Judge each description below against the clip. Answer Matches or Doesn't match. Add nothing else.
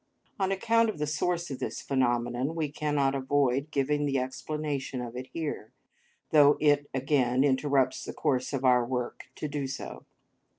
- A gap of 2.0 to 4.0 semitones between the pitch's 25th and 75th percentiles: Matches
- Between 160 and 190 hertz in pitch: Doesn't match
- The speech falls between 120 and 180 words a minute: Matches